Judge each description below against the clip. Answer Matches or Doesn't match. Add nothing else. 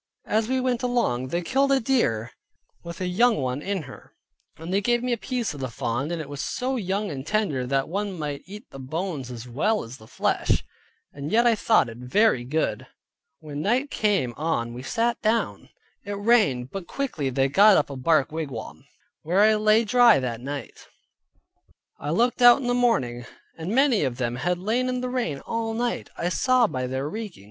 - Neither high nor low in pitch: Matches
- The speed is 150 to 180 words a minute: Doesn't match